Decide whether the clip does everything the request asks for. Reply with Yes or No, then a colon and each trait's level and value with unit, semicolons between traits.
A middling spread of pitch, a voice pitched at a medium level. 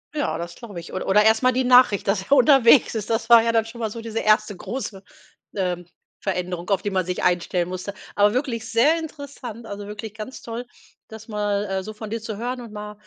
No: average, 3.0 semitones; high, 215 Hz